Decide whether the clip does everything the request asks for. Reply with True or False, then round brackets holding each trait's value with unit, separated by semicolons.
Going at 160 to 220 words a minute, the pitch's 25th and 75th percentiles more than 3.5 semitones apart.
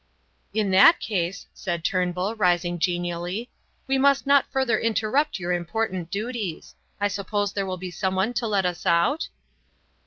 False (150 wpm; 4.1 semitones)